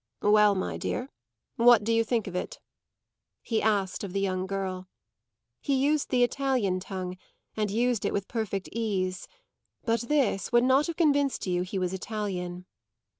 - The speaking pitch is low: No, high, 210 Hz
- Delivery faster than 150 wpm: Yes, average, 165 wpm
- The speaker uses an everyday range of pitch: Yes, average, 4.6 semitones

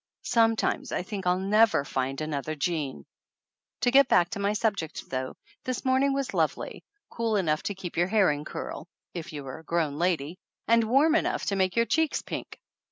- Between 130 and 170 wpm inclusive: No, average, 195 wpm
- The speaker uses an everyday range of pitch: No, wide, 6.6 semitones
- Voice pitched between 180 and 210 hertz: Yes, medium, 185 Hz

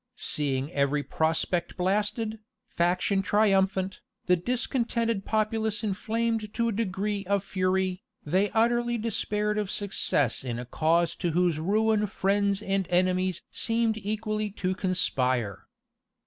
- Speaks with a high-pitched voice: Yes, high, 195 Hz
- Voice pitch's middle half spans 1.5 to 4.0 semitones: Yes, average, 3.3 semitones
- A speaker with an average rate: No, slow, 120 wpm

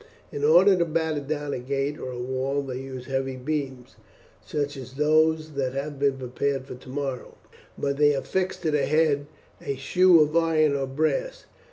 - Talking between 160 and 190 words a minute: Yes, average, 180 wpm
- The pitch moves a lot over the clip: No, average, 2.7 semitones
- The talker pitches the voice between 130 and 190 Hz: Yes, medium, 140 Hz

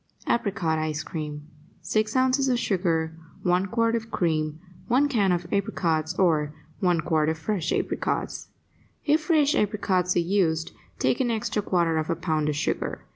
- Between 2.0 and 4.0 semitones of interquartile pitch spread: No, average, 5.3 semitones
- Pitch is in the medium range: Yes, medium, 180 Hz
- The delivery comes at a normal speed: Yes, average, 160 wpm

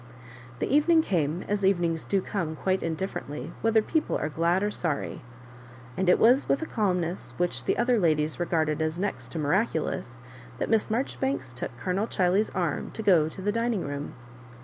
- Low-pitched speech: No, medium, 180 Hz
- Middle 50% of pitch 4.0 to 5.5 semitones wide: Yes, average, 5.2 semitones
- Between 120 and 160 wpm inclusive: No, average, 175 wpm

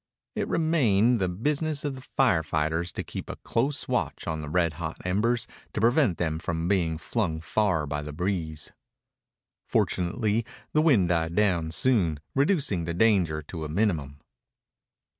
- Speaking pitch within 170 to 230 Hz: No, very low, 90 Hz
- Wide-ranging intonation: Yes, wide, 6.4 semitones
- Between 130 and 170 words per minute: Yes, average, 160 wpm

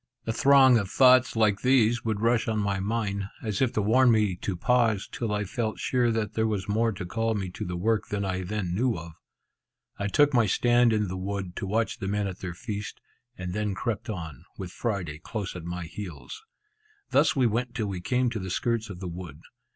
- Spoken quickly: Yes, fast, 220 wpm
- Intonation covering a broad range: No, average, 3.6 semitones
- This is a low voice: Yes, low, 105 Hz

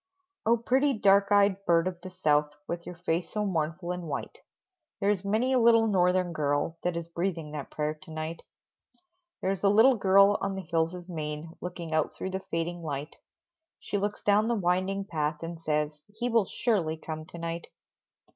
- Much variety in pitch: No, average, 3.7 semitones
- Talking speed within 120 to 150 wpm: No, average, 190 wpm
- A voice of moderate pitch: Yes, medium, 180 Hz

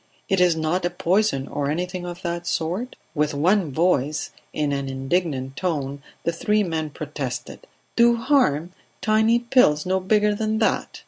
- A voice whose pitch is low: No, medium, 175 Hz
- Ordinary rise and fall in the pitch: No, wide, 5.7 semitones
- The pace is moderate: Yes, average, 155 wpm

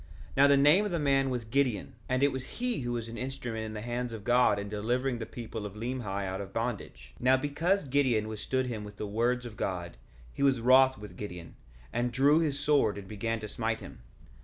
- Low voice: Yes, low, 120 Hz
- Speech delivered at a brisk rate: Yes, fast, 235 wpm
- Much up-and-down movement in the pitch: No, average, 4.1 semitones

